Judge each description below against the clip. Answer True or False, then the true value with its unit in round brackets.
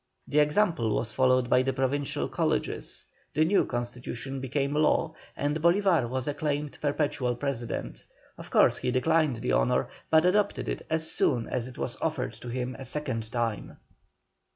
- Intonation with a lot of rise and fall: False (3.6 semitones)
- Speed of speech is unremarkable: True (160 wpm)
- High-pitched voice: False (135 Hz)